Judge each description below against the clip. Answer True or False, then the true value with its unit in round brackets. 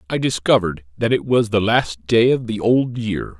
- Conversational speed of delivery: False (210 wpm)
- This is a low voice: True (110 Hz)